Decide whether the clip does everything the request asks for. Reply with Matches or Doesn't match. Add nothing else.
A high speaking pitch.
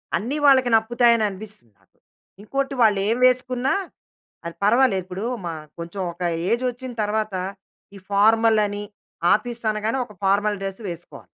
Matches